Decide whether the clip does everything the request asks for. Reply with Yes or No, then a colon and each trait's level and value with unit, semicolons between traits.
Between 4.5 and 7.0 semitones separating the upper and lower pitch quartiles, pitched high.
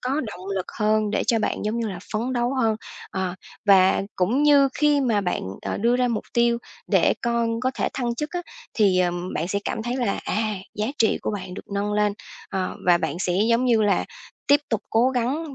No: average, 3.8 semitones; high, 225 Hz